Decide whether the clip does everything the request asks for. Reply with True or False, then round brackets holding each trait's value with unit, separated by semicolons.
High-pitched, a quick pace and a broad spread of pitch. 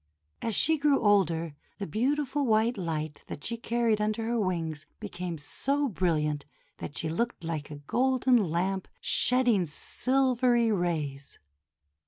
False (205 Hz; 135 wpm; 7.0 semitones)